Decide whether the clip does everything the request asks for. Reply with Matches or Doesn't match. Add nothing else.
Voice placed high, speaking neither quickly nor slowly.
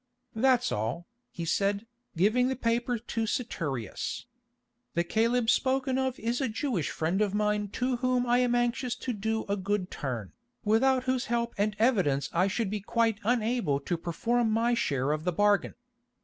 Matches